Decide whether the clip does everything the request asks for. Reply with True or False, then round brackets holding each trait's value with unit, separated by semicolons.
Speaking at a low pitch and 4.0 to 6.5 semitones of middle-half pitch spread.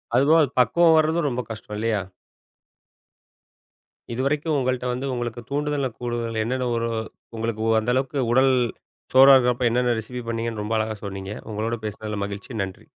False (120 Hz; 3.1 semitones)